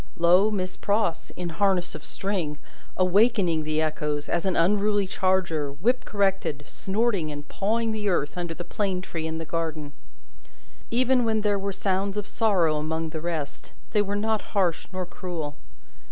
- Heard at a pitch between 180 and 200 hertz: Yes, medium, 185 Hz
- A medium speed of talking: Yes, average, 165 wpm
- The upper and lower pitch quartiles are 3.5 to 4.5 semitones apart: Yes, average, 4.1 semitones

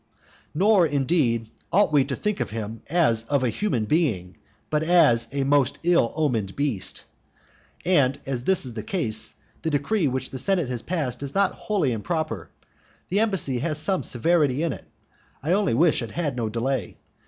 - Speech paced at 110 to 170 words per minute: No, average, 180 wpm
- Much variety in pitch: Yes, wide, 6.3 semitones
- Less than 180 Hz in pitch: Yes, medium, 140 Hz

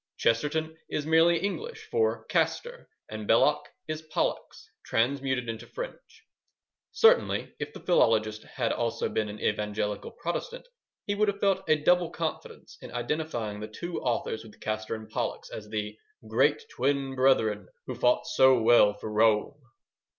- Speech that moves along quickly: No, average, 150 wpm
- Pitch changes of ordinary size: No, wide, 7.3 semitones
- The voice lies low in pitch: Yes, low, 130 Hz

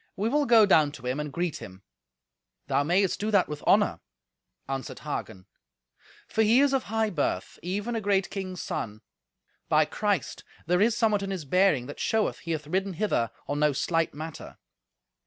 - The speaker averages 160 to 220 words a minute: Yes, average, 180 wpm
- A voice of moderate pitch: Yes, medium, 180 Hz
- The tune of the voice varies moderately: No, wide, 6.1 semitones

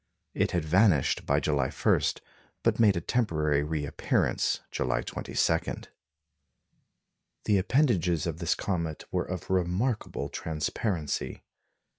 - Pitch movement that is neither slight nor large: Yes, average, 4.1 semitones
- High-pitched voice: No, very low, 85 Hz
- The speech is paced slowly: Yes, slow, 110 wpm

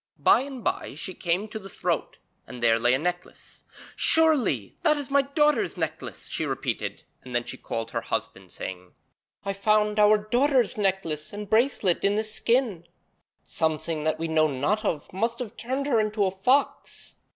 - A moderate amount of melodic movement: No, wide, 7.1 semitones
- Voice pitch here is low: No, high, 200 Hz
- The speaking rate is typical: Yes, average, 180 wpm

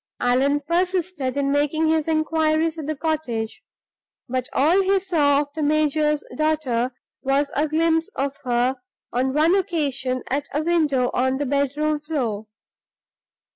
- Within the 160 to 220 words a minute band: No, average, 140 wpm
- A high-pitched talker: Yes, very high, 295 Hz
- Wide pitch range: No, average, 3.1 semitones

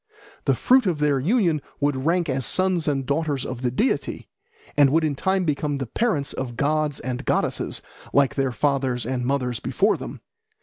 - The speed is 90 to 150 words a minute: No, average, 180 wpm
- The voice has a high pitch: No, medium, 140 Hz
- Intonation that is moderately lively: Yes, average, 3.6 semitones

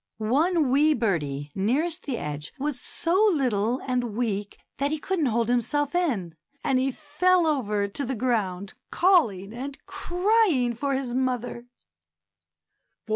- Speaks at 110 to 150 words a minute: Yes, slow, 135 wpm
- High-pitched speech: Yes, very high, 255 Hz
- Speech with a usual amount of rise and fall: No, wide, 5.9 semitones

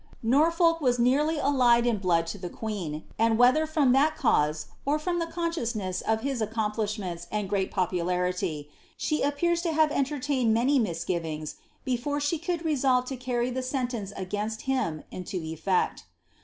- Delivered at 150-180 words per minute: Yes, average, 160 wpm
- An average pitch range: No, wide, 7.4 semitones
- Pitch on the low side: No, high, 240 Hz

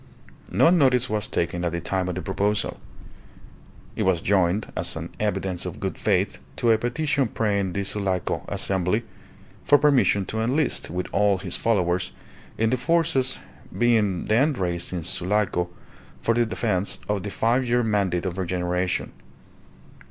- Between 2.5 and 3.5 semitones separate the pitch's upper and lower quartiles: No, average, 4.4 semitones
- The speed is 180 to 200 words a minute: No, average, 155 wpm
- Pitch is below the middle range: Yes, low, 100 Hz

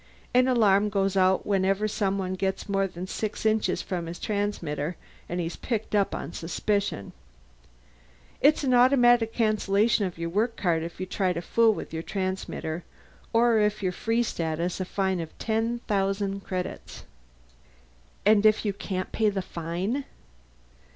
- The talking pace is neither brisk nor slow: Yes, average, 155 wpm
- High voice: Yes, high, 195 Hz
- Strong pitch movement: No, average, 3.1 semitones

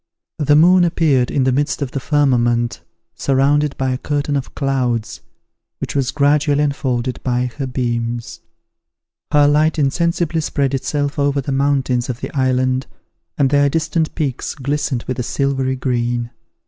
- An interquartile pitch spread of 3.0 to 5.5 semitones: No, narrow, 2.4 semitones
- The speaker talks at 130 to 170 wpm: Yes, average, 150 wpm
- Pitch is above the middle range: No, low, 135 Hz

